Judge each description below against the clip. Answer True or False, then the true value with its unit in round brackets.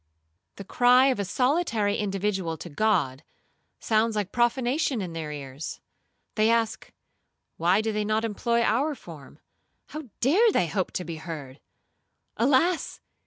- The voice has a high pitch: True (215 Hz)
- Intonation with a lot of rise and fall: True (5.9 semitones)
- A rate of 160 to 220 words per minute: False (140 wpm)